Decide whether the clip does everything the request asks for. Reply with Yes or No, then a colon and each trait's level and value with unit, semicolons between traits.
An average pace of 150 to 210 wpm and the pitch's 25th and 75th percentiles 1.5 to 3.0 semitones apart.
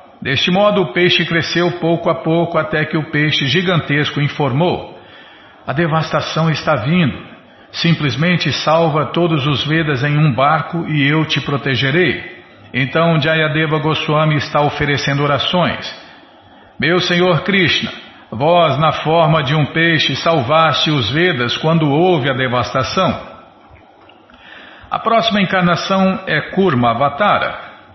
No: average, 125 wpm; average, 2.7 semitones